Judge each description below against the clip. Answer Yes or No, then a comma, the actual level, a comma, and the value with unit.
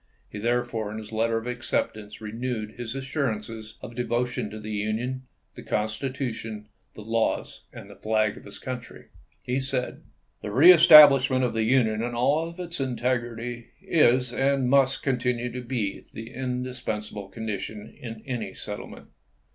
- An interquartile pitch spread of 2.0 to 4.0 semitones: Yes, average, 2.9 semitones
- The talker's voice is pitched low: Yes, low, 120 Hz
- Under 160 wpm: Yes, average, 145 wpm